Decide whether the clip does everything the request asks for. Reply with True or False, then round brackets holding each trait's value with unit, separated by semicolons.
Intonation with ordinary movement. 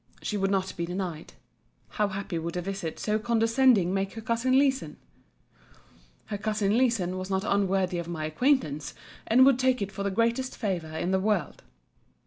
True (4.1 semitones)